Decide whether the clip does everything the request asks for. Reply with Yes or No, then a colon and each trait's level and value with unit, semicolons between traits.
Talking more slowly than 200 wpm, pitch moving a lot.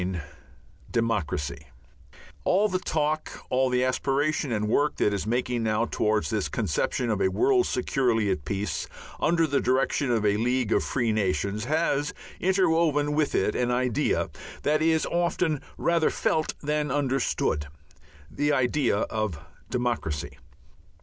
Yes: average, 140 wpm; wide, 5.8 semitones